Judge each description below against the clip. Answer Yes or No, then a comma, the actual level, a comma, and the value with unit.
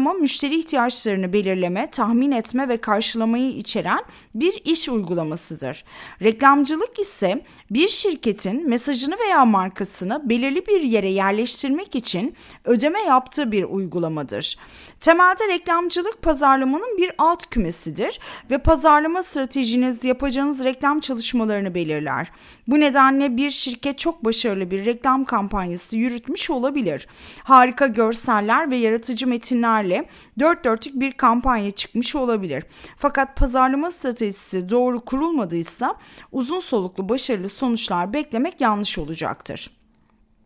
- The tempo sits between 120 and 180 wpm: No, average, 110 wpm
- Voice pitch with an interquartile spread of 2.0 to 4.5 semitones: No, average, 5.1 semitones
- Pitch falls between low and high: No, very high, 250 Hz